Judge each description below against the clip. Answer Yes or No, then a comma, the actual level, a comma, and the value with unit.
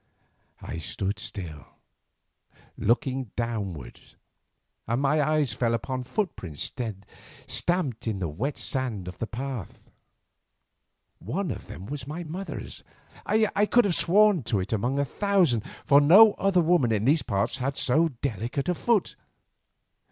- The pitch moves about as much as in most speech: No, wide, 7.4 semitones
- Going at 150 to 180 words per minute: No, slow, 135 wpm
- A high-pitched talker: No, low, 135 Hz